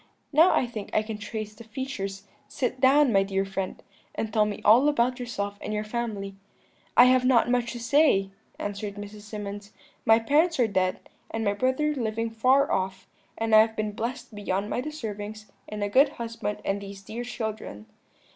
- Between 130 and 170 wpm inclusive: No, average, 185 wpm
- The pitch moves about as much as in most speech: Yes, average, 3.3 semitones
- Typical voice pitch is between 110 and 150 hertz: No, high, 220 Hz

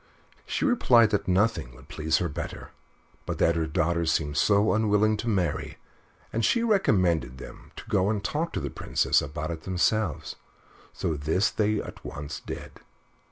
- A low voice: Yes, very low, 95 Hz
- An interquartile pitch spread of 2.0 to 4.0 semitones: No, wide, 5.5 semitones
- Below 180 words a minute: Yes, average, 165 wpm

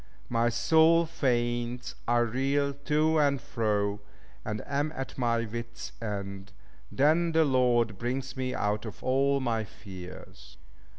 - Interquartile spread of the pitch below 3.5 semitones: No, average, 4.2 semitones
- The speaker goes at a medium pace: No, slow, 130 wpm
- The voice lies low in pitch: Yes, low, 120 Hz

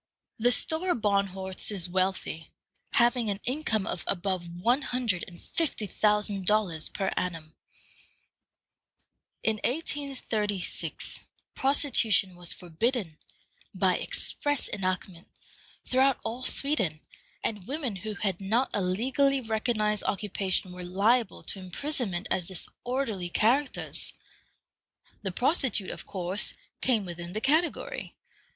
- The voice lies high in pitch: Yes, high, 210 Hz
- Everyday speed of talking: No, slow, 110 wpm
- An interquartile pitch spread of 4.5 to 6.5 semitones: Yes, average, 5.2 semitones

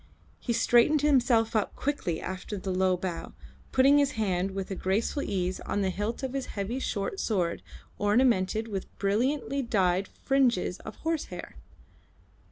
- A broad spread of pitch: Yes, wide, 5.7 semitones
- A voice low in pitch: No, high, 215 Hz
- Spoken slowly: No, average, 150 wpm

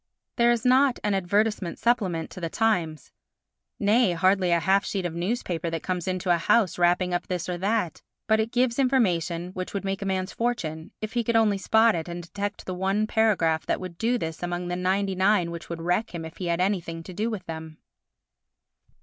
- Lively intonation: No, average, 3.9 semitones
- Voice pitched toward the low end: No, medium, 185 Hz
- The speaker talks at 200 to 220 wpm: Yes, fast, 205 wpm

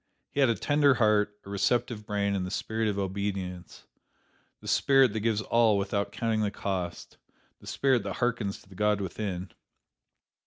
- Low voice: Yes, low, 105 Hz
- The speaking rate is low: No, average, 170 wpm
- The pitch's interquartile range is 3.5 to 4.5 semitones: No, average, 2.7 semitones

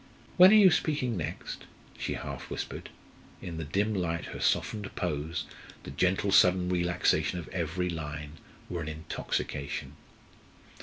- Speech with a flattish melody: No, average, 3.7 semitones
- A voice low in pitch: Yes, very low, 85 Hz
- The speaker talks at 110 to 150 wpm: Yes, average, 140 wpm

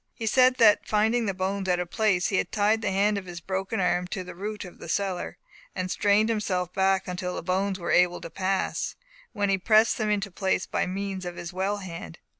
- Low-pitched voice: No, high, 195 Hz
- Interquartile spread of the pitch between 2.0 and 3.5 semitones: Yes, narrow, 2.4 semitones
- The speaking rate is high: Yes, fast, 230 wpm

